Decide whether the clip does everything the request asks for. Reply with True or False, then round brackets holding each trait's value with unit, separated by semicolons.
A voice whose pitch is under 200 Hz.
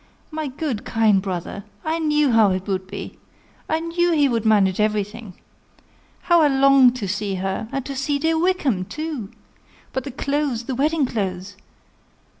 False (250 Hz)